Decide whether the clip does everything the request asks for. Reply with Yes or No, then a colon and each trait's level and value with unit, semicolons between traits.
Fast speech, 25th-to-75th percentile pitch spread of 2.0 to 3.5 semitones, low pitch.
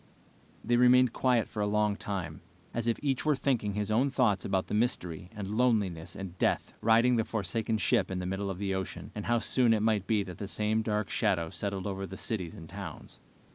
Yes: fast, 215 wpm; average, 3.2 semitones; low, 105 Hz